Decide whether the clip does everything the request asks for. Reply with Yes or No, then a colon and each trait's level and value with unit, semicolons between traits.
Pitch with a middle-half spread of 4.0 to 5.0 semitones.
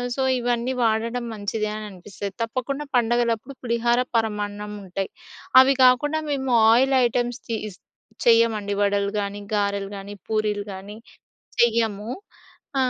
No: average, 2.8 semitones